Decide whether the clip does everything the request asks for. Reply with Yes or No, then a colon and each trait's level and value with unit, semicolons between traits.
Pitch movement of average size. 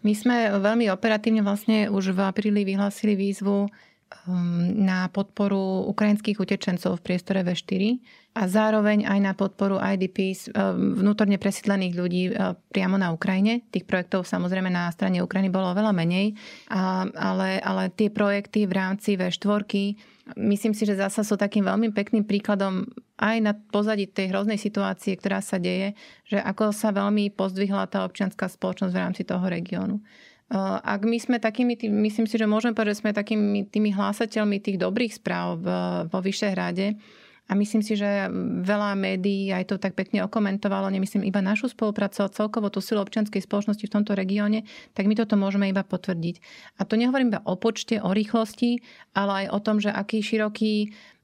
No: narrow, 1.8 semitones